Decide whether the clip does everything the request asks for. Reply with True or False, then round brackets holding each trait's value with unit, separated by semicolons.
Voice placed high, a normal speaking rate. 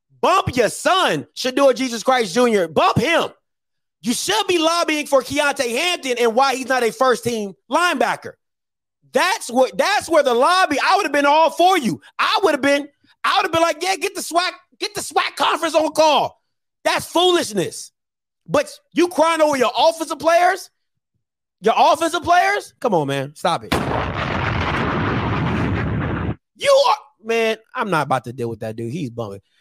True (290 Hz; 175 wpm)